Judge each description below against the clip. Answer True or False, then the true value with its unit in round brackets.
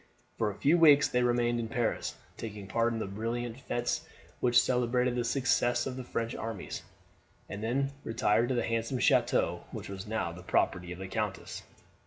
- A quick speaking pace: False (190 wpm)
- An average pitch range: False (2.3 semitones)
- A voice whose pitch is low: True (115 Hz)